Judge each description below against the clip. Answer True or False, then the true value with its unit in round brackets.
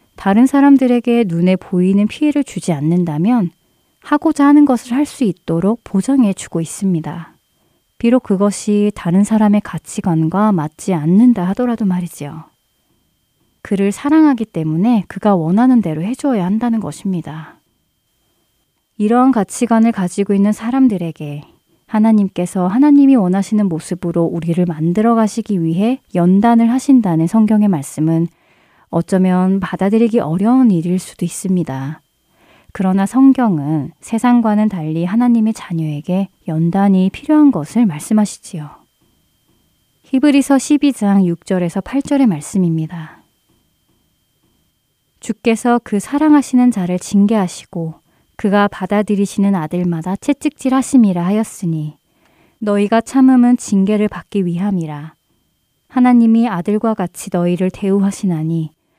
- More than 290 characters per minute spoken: True (300 characters per minute)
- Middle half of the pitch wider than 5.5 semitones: False (5.2 semitones)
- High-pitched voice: True (200 Hz)